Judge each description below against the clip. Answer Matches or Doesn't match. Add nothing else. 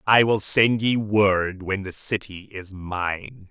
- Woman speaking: Doesn't match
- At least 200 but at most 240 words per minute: Doesn't match